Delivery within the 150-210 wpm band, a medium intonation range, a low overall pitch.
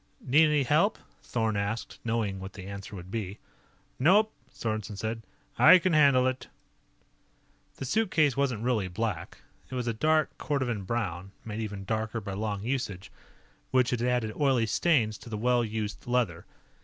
Yes: average, 160 wpm; average, 4.0 semitones; low, 115 Hz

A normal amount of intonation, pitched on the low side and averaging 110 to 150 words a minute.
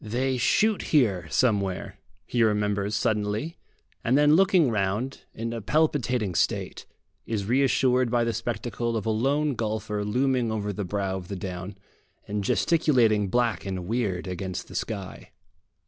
Yes: average, 3.9 semitones; low, 110 Hz; average, 145 wpm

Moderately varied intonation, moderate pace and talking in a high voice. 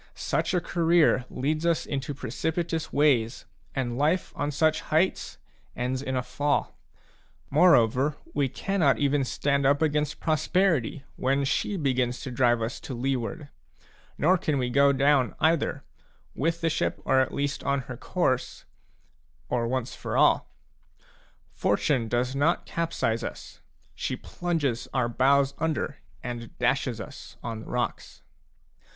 No: average, 3.7 semitones; average, 150 wpm; medium, 140 Hz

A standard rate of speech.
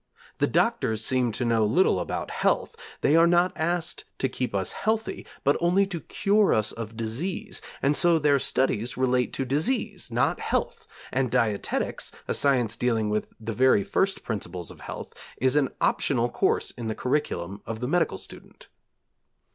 Yes: average, 170 wpm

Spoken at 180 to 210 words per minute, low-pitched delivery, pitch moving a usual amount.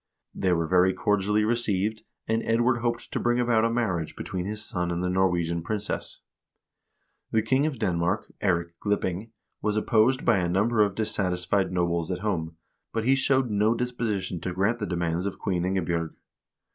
No: average, 170 wpm; low, 100 Hz; average, 4.1 semitones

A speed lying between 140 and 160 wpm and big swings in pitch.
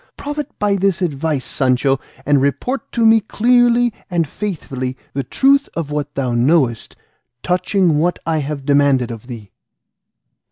Yes: average, 145 wpm; wide, 7.4 semitones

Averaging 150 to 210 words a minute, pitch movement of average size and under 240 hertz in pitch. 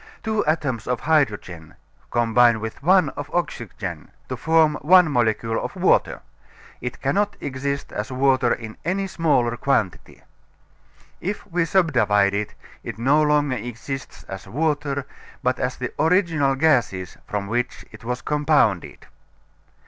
No: slow, 135 wpm; average, 5.0 semitones; low, 135 Hz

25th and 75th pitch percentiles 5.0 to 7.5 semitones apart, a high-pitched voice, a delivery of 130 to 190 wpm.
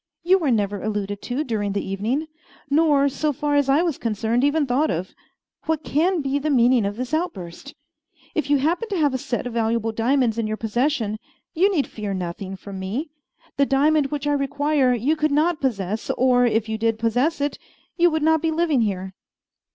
No: wide, 5.5 semitones; very high, 265 Hz; average, 200 wpm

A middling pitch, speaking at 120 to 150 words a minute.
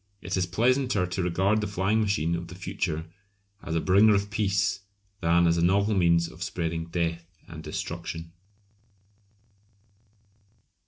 No: very low, 90 Hz; average, 145 wpm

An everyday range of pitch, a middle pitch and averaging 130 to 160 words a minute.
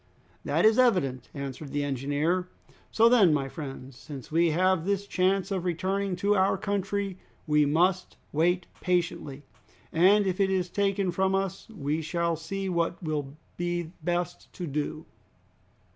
Yes: average, 4.0 semitones; medium, 175 Hz; average, 150 wpm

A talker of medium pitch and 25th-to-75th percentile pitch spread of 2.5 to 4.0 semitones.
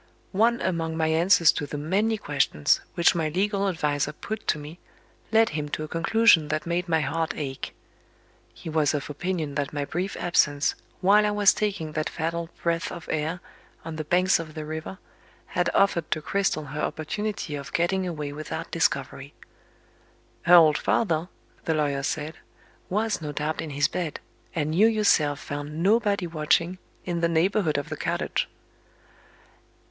Yes: medium, 165 Hz; average, 3.7 semitones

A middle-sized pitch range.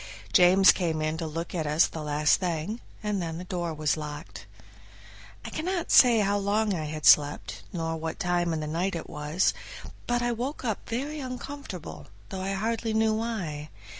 No: wide, 5.7 semitones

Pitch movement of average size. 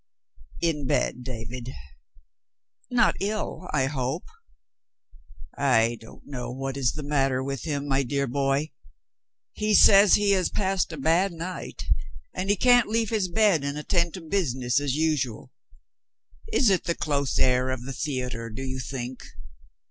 No: wide, 5.8 semitones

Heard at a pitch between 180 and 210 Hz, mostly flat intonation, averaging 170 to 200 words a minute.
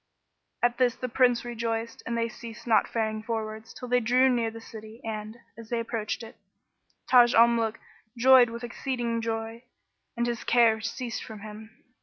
No: high, 230 Hz; narrow, 1.3 semitones; average, 175 wpm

